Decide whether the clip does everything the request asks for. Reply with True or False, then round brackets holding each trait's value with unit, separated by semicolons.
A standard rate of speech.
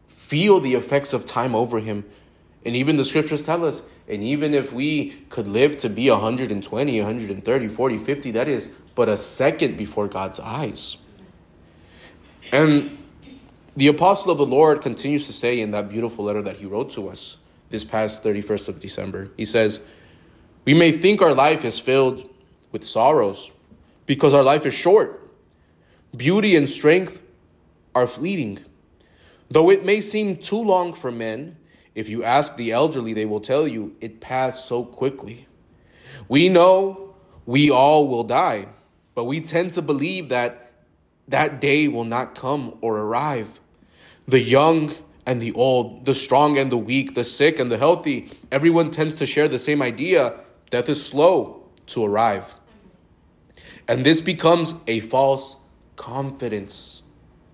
True (155 wpm)